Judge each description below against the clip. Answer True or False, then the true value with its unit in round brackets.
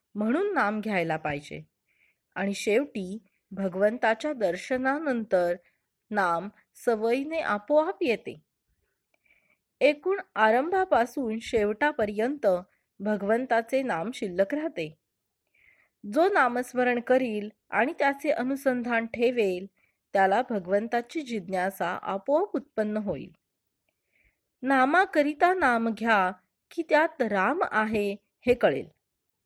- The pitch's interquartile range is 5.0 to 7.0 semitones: True (5.3 semitones)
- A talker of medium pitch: False (230 Hz)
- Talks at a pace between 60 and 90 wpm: True (85 wpm)